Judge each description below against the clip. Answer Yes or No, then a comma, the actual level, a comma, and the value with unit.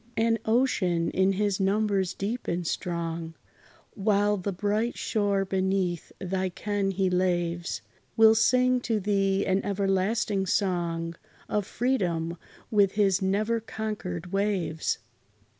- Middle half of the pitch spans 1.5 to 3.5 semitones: Yes, average, 2.7 semitones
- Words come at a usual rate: No, slow, 120 wpm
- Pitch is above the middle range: Yes, high, 195 Hz